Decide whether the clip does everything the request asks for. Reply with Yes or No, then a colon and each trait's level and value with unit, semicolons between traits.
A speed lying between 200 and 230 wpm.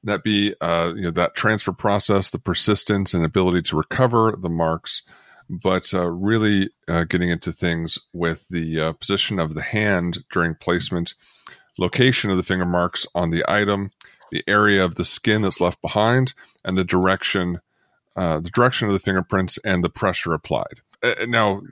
No: average, 175 wpm